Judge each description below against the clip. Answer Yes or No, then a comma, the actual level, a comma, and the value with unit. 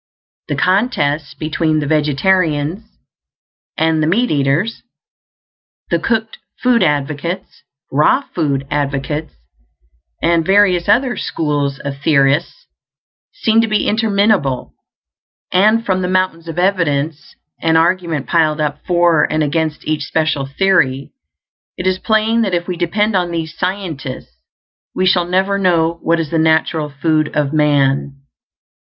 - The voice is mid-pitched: Yes, medium, 165 Hz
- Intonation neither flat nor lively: Yes, average, 4.1 semitones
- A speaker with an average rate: No, slow, 130 wpm